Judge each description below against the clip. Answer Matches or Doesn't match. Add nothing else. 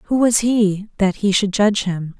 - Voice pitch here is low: Doesn't match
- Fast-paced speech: Matches